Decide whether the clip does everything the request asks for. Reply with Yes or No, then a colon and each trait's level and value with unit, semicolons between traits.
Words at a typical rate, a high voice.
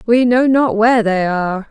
No: fast, 210 wpm; high, 220 Hz